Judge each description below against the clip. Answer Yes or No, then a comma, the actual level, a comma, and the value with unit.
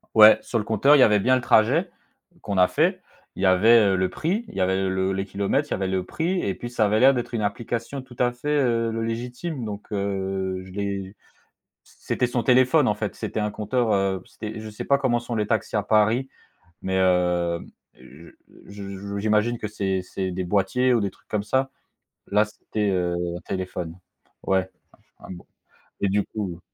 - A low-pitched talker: Yes, low, 105 Hz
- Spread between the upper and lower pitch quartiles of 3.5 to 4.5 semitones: Yes, average, 3.9 semitones